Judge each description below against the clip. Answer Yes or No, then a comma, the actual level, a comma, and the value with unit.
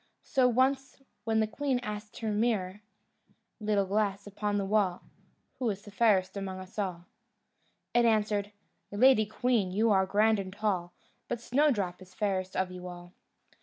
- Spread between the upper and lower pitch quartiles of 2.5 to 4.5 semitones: Yes, average, 2.8 semitones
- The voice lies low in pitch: No, high, 205 Hz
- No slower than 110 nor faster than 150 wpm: No, average, 160 wpm